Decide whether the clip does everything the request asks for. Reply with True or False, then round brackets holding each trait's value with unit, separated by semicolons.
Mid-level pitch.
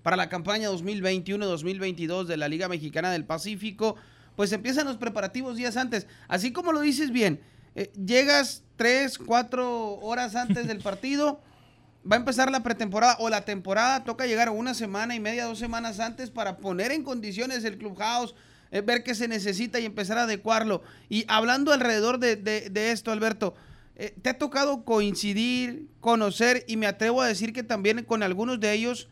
False (225 Hz)